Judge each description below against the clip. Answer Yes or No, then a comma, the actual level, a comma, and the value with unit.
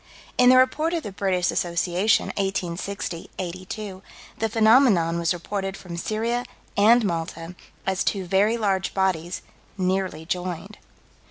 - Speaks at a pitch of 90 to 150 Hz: No, high, 190 Hz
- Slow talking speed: Yes, slow, 125 wpm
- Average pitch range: Yes, average, 3.4 semitones